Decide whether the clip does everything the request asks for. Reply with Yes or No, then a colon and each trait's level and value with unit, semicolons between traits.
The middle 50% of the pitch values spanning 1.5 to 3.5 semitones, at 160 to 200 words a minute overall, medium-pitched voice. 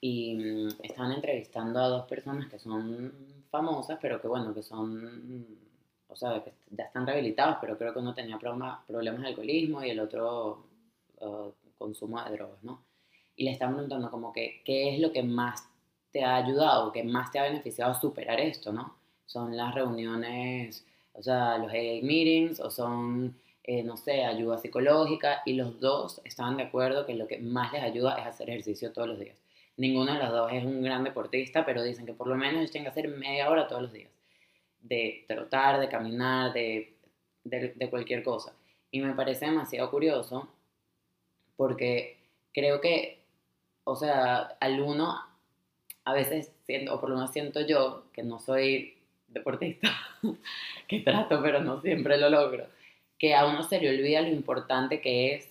No: average, 3.0 semitones; average, 180 wpm; low, 125 Hz